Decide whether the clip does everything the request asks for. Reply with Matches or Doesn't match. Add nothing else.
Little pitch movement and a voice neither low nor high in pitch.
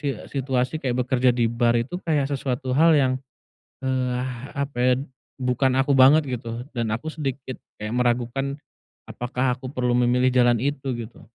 Doesn't match